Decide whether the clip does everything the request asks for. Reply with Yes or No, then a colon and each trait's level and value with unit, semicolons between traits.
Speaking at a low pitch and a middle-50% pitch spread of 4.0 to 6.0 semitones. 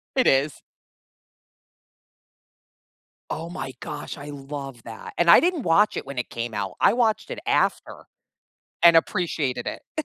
No: medium, 150 Hz; average, 4.8 semitones